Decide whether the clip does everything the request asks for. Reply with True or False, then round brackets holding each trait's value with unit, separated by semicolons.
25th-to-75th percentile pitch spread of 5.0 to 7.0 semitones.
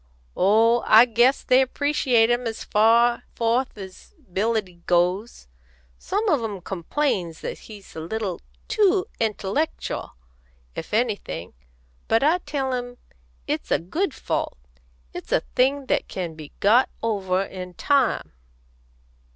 True (5.4 semitones)